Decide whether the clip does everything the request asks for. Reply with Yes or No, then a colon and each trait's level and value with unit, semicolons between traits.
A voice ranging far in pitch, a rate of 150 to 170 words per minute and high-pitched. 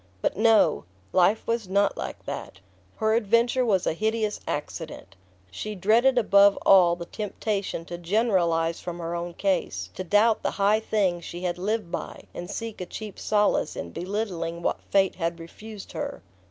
No: average, 3.9 semitones; average, 165 wpm; high, 195 Hz